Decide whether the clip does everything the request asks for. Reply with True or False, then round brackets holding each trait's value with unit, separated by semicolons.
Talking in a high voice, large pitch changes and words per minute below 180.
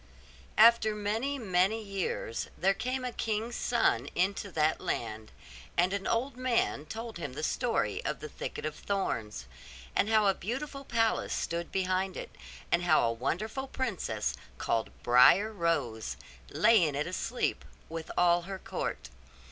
True (195 Hz; 6.5 semitones; 150 wpm)